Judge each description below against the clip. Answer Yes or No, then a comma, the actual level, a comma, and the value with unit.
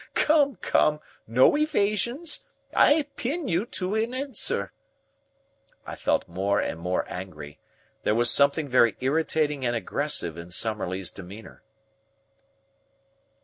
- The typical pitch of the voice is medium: No, low, 130 Hz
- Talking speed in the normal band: No, slow, 115 wpm